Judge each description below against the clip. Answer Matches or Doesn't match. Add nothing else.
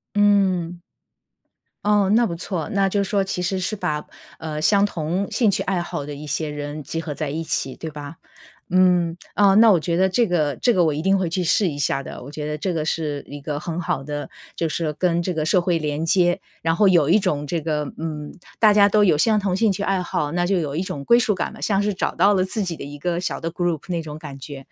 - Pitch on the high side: Doesn't match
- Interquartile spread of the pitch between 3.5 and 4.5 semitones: Matches